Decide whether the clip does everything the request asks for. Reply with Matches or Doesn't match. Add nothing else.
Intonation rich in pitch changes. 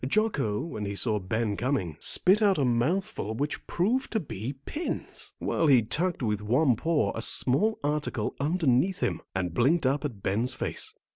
Matches